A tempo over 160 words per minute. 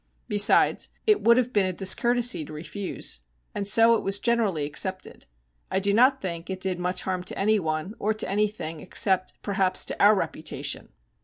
Yes: average, 175 wpm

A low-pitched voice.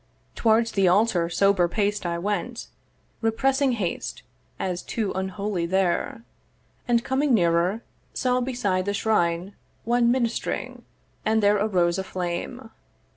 No: high, 205 Hz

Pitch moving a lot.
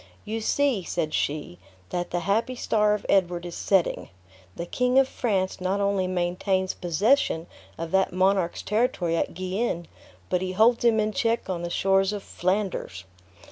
No: average, 3.5 semitones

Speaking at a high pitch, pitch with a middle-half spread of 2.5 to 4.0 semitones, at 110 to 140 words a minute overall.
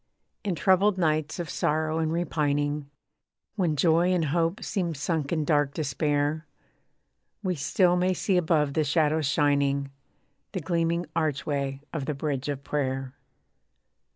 No: medium, 155 Hz; average, 2.9 semitones; slow, 135 wpm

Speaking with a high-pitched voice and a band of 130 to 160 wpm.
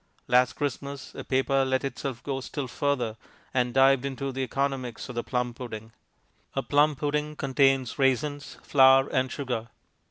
No: low, 135 Hz; average, 155 wpm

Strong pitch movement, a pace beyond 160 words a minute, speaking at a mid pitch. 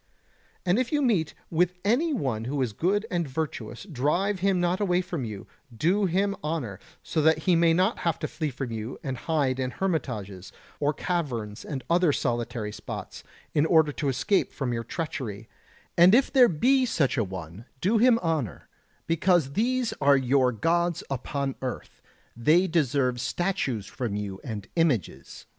Yes: wide, 6.7 semitones; average, 170 wpm; medium, 150 Hz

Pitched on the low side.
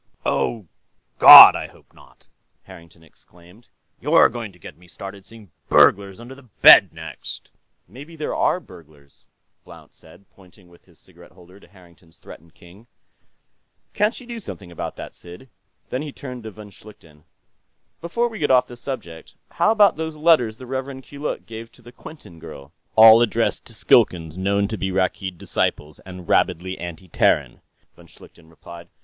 Yes: low, 100 Hz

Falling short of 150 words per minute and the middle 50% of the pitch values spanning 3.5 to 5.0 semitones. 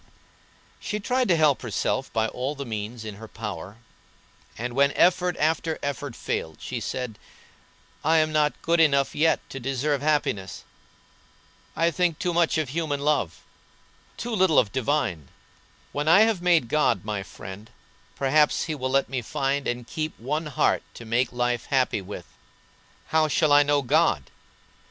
No: average, 160 wpm; average, 4.7 semitones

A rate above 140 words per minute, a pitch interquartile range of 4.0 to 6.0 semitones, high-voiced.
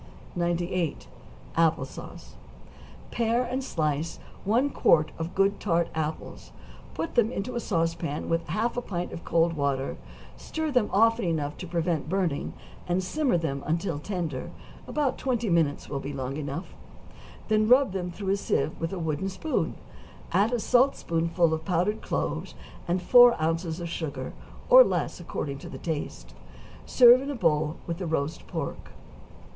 No: average, 160 wpm; average, 5.2 semitones; medium, 175 Hz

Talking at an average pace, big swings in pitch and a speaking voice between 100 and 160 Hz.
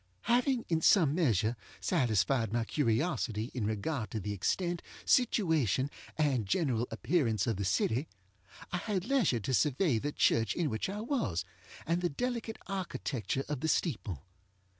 Yes: average, 150 wpm; wide, 8.1 semitones; medium, 140 Hz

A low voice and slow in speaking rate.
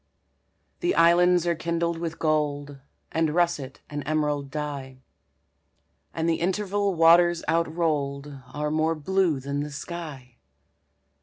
No: medium, 160 Hz; slow, 120 wpm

